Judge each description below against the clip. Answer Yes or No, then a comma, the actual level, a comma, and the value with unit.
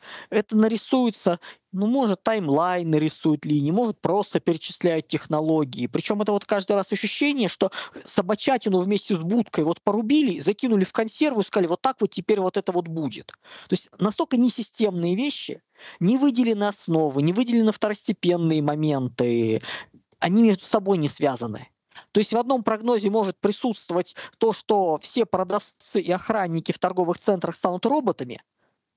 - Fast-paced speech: No, average, 150 wpm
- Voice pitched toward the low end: No, high, 200 Hz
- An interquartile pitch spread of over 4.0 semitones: Yes, average, 4.5 semitones